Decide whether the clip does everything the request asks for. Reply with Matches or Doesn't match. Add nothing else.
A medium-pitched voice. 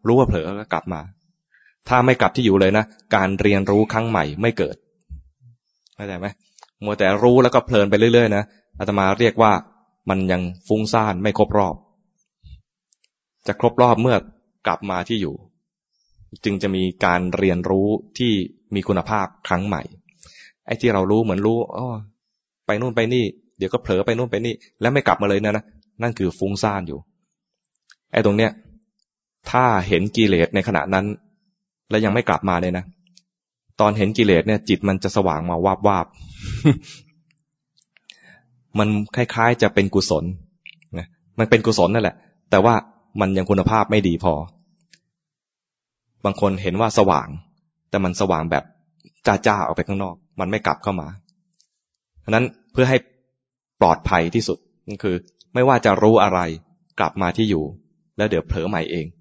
Doesn't match